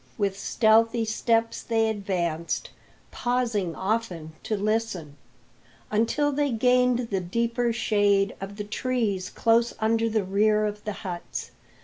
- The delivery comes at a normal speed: No, slow, 125 wpm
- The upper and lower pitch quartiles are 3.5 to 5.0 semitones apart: No, average, 2.7 semitones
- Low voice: No, high, 220 Hz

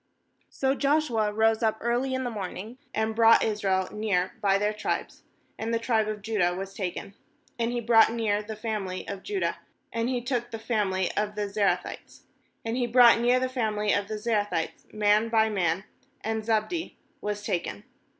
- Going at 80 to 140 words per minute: No, average, 180 wpm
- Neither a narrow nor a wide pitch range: No, narrow, 2.2 semitones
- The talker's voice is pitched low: No, high, 220 Hz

